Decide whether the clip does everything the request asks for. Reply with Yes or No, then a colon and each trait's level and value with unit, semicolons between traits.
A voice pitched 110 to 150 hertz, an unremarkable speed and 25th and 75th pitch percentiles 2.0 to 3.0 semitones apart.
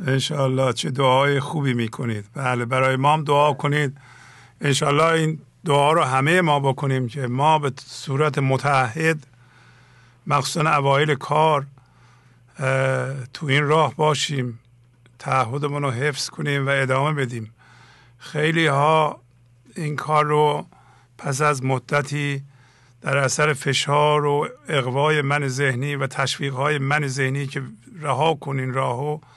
No: medium, 140 Hz; slow, 125 wpm; narrow, 2.4 semitones